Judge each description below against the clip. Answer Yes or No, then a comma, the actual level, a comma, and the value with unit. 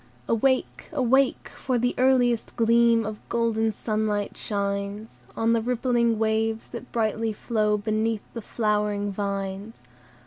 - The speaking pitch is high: Yes, high, 225 Hz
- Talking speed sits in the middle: No, slow, 125 wpm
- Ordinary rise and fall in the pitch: No, narrow, 1.9 semitones